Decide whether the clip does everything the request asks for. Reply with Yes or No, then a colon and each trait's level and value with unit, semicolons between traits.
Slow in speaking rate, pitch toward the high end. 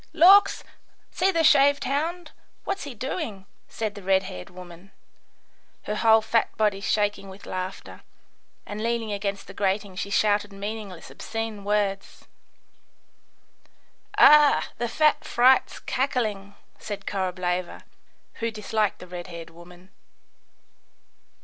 Yes: slow, 125 wpm; high, 205 Hz